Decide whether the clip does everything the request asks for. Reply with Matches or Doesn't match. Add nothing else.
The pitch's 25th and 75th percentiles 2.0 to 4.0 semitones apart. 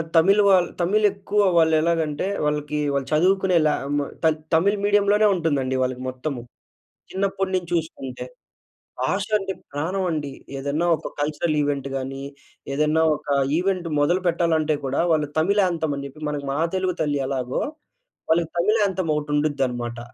Doesn't match